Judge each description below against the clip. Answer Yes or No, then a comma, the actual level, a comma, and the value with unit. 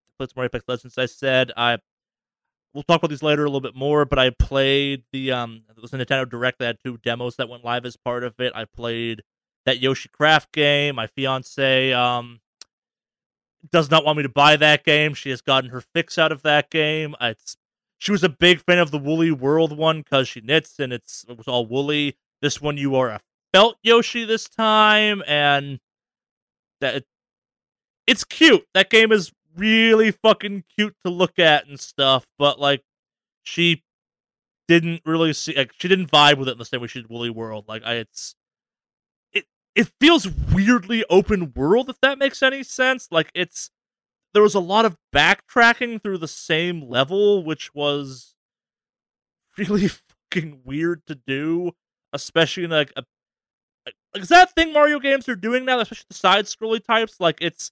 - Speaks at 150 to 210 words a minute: Yes, average, 190 wpm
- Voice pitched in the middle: Yes, medium, 150 Hz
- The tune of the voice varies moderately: No, wide, 6.9 semitones